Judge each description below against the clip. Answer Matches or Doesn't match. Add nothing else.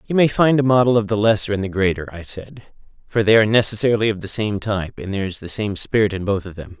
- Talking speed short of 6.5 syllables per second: Doesn't match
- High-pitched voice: Doesn't match